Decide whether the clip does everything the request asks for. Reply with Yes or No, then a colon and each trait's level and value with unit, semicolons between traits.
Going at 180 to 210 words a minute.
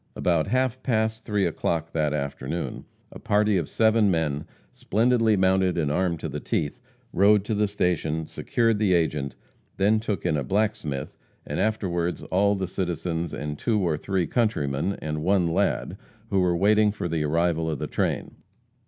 No: average, 170 wpm